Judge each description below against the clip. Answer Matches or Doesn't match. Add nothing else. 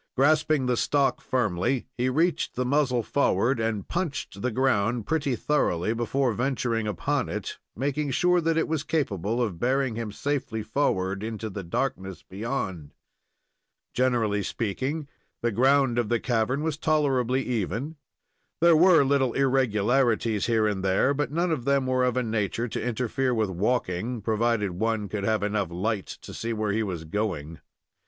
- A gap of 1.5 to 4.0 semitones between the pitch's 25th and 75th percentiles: Doesn't match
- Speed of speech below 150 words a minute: Doesn't match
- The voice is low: Matches